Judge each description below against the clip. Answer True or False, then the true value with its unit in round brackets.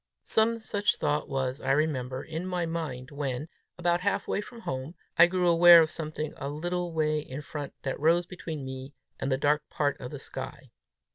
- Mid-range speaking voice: True (155 Hz)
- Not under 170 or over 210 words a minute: True (190 wpm)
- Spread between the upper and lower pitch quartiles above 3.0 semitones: True (4.0 semitones)